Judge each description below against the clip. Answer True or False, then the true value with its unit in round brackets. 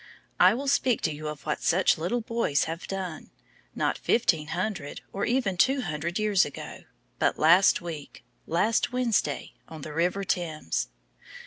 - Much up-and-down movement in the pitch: True (5.7 semitones)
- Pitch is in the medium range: True (175 Hz)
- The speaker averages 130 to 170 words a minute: True (155 wpm)